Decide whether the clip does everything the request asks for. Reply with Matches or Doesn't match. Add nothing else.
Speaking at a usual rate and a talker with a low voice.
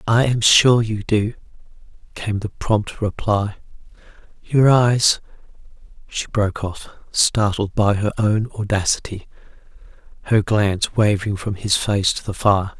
Doesn't match